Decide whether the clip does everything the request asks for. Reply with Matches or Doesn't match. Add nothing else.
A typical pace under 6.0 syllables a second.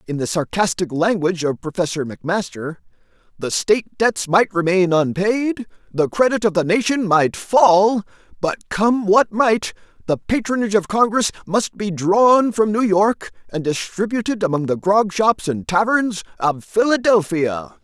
Matches